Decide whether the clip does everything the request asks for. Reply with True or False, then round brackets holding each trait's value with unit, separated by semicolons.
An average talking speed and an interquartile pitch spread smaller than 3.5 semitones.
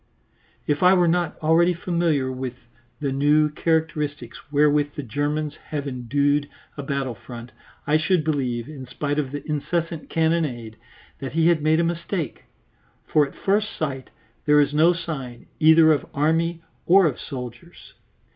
True (155 wpm; 2.9 semitones)